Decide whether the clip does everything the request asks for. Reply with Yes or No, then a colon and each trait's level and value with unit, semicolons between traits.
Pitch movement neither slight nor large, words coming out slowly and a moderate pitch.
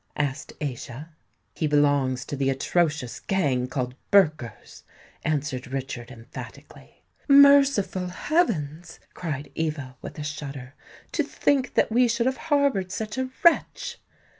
No: wide, 8.1 semitones; slow, 125 wpm; medium, 150 Hz